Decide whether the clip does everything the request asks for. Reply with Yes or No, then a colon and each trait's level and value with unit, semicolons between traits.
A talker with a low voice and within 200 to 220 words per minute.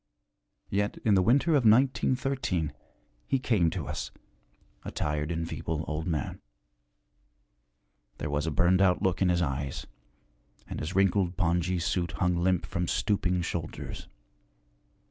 No: very low, 90 Hz; average, 140 wpm